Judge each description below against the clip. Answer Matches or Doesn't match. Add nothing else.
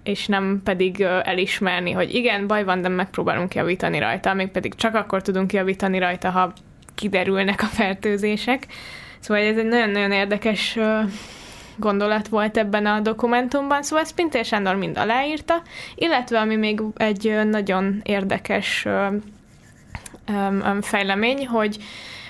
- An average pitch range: Doesn't match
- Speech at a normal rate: Matches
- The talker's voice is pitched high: Matches